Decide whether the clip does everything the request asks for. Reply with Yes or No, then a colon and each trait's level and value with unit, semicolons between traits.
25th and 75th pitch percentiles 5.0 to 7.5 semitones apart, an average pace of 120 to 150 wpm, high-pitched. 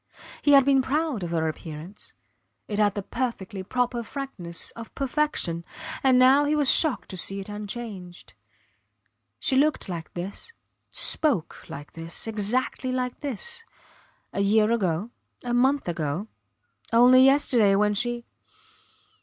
Yes: wide, 5.6 semitones; slow, 135 wpm; high, 230 Hz